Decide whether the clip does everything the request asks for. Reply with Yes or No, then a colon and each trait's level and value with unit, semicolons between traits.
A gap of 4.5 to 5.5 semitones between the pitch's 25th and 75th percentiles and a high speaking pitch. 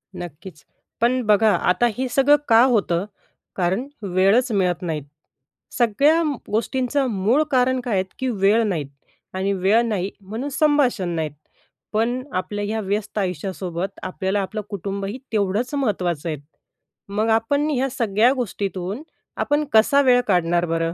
Yes: average, 4.9 semitones; high, 210 Hz